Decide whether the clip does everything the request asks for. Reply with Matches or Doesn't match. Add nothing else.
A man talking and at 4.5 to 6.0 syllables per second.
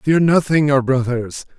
Doesn't match